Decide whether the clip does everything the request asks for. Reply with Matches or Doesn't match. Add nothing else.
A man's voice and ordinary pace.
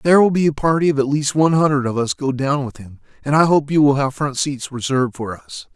Doesn't match